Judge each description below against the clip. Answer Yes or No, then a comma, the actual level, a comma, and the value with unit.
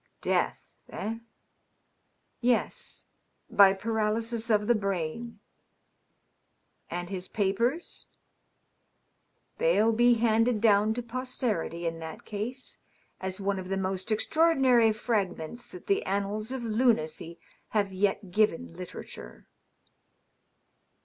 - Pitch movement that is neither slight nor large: Yes, average, 3.5 semitones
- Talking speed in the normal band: No, slow, 120 wpm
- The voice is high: Yes, high, 215 Hz